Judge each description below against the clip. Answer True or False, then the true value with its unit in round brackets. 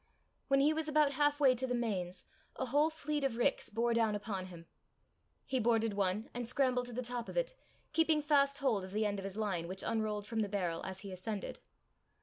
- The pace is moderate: False (220 wpm)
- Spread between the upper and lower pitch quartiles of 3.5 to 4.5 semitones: False (5.5 semitones)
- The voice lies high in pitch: True (230 Hz)